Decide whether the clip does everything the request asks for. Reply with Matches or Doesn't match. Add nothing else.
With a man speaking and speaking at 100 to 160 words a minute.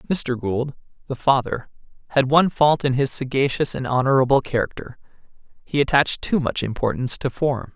Matches